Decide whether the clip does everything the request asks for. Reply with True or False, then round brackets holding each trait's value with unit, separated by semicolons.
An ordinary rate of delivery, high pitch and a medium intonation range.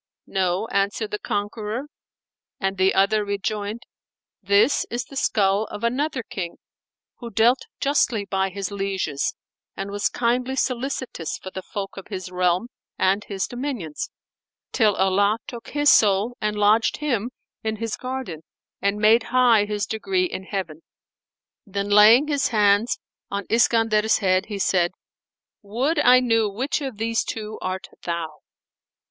True (145 wpm; 210 Hz; 3.4 semitones)